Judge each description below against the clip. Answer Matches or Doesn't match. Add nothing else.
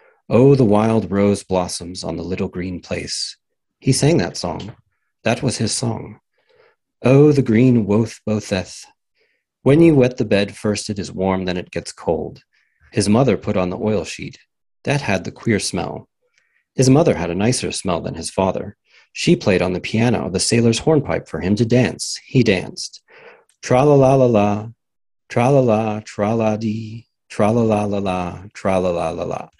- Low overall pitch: Matches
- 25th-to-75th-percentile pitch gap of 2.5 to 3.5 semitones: Doesn't match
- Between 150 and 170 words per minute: Matches